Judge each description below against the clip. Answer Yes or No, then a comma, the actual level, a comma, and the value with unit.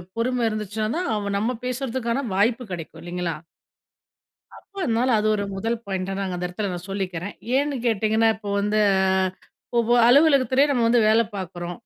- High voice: Yes, high, 215 Hz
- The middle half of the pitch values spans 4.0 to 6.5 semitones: Yes, average, 4.3 semitones